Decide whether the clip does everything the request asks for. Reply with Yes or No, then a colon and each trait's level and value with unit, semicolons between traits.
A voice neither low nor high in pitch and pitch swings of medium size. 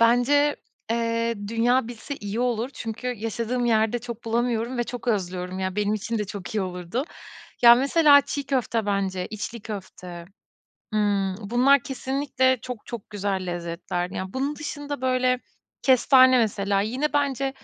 No: high, 230 Hz; average, 4.2 semitones